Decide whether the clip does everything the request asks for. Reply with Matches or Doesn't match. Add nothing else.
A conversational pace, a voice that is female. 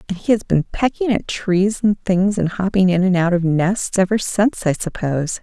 Doesn't match